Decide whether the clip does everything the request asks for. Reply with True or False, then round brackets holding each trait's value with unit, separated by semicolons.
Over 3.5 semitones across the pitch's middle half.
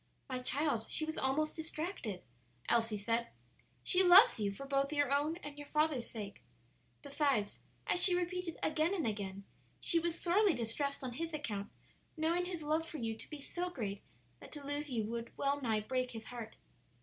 True (5.6 semitones)